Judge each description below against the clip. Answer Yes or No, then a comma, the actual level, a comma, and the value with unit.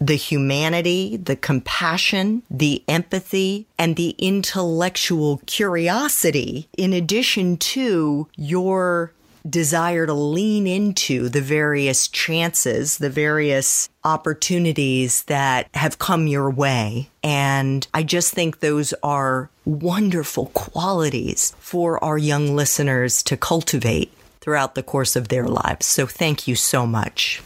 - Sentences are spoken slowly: Yes, slow, 120 wpm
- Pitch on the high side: No, medium, 155 Hz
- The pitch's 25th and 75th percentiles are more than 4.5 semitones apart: No, average, 4.1 semitones